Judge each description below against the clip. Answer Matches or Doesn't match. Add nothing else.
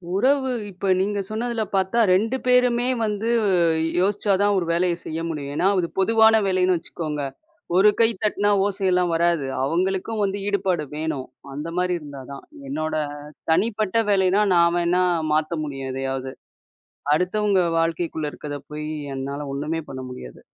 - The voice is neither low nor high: Matches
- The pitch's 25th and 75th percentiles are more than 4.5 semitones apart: Matches